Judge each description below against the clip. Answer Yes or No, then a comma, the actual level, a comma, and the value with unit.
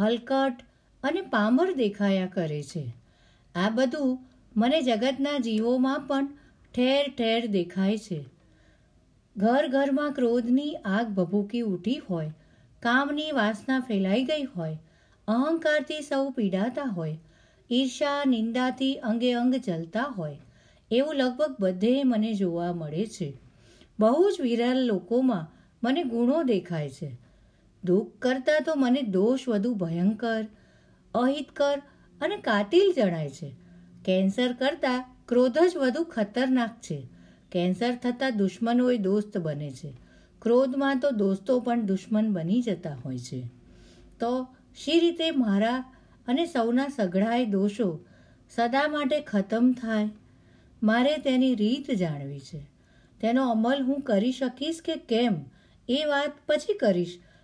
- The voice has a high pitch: Yes, high, 235 Hz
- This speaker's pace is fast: No, average, 120 wpm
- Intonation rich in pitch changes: Yes, wide, 6.0 semitones